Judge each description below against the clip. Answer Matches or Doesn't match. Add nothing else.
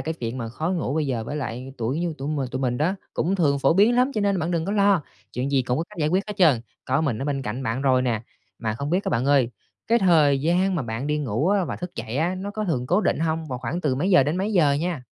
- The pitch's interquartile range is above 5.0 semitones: Matches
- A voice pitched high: Doesn't match